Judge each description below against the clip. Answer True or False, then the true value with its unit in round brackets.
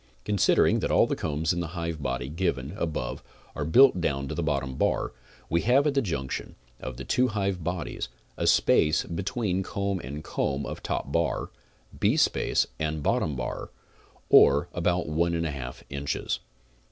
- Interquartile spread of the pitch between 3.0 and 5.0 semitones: True (4.6 semitones)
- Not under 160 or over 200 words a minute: True (170 wpm)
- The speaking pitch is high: False (80 Hz)